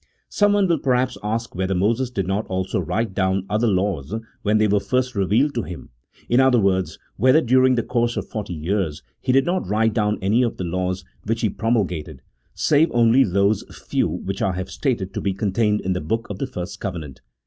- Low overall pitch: Yes, low, 105 Hz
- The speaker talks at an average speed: No, fast, 215 wpm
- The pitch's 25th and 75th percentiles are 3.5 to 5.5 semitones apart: Yes, average, 4.4 semitones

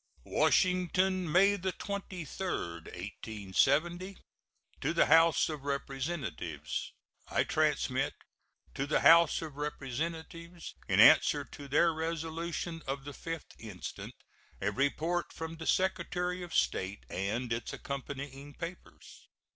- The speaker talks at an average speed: No, slow, 110 wpm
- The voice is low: No, medium, 160 Hz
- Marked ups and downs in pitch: No, average, 4.3 semitones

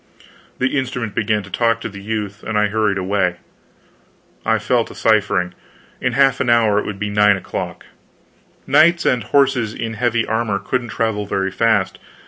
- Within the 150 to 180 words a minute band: Yes, average, 170 wpm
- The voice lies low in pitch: Yes, low, 110 Hz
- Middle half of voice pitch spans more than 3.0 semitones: No, narrow, 2.6 semitones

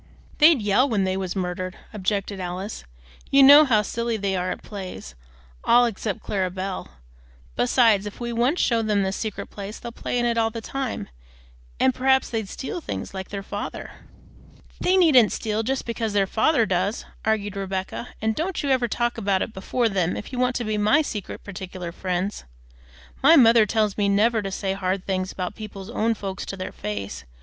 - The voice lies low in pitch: No, high, 210 Hz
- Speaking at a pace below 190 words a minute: No, average, 195 wpm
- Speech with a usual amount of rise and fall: Yes, average, 3.7 semitones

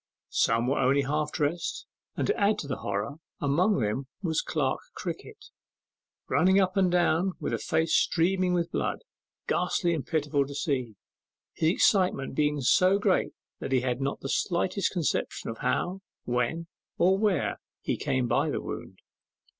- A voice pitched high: No, medium, 160 Hz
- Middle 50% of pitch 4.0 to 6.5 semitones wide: Yes, average, 5.2 semitones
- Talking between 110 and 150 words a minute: No, average, 160 wpm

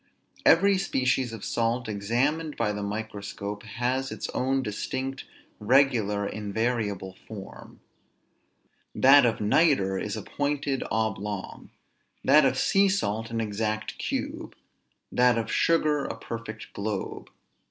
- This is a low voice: Yes, low, 115 Hz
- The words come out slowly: Yes, slow, 120 wpm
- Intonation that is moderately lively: Yes, average, 4.4 semitones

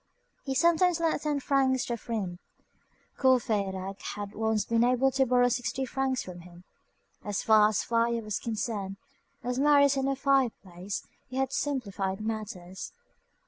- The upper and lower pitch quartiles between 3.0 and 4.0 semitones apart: No, average, 4.7 semitones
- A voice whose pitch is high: Yes, high, 235 Hz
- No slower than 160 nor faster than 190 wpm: No, average, 150 wpm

